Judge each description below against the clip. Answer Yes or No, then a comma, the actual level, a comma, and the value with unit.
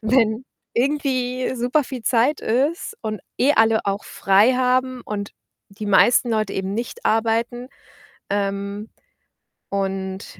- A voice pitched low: No, high, 230 Hz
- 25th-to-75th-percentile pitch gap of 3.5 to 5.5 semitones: Yes, average, 3.9 semitones